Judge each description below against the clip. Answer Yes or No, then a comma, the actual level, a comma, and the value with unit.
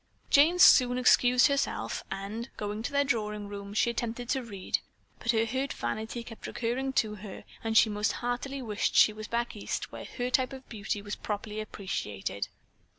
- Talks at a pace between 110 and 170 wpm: No, average, 180 wpm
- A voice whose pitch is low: No, high, 225 Hz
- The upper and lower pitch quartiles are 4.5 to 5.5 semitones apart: No, average, 3.1 semitones